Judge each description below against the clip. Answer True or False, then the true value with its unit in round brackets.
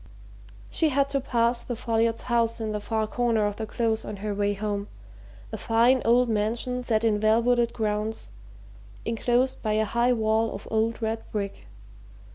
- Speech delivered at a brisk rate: False (175 wpm)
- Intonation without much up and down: True (1.8 semitones)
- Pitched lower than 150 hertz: False (225 Hz)